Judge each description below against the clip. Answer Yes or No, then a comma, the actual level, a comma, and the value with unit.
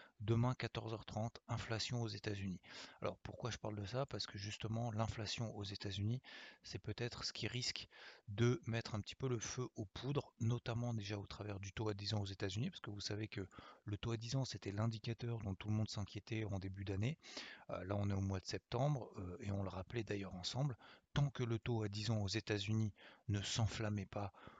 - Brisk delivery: No, average, 210 wpm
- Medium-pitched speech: No, low, 110 Hz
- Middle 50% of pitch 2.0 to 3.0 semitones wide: Yes, narrow, 2.4 semitones